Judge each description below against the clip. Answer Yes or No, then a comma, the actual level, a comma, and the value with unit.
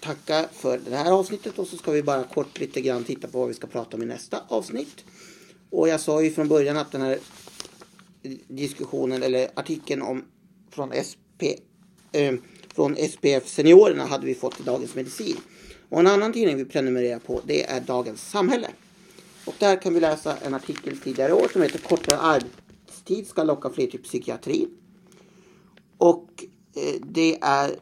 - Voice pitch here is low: No, medium, 160 Hz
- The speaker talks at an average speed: Yes, average, 175 wpm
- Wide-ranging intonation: Yes, wide, 6.1 semitones